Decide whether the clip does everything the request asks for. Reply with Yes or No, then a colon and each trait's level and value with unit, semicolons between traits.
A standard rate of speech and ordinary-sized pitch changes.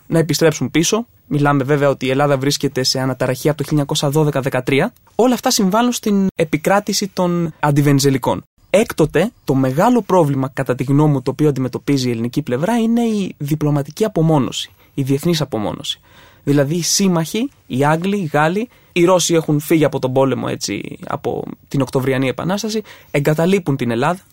Yes: average, 160 wpm; average, 4.8 semitones